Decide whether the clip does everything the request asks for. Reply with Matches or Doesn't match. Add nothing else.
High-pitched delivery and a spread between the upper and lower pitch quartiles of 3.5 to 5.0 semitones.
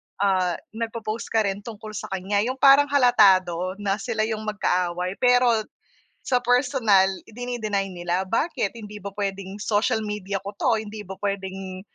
Doesn't match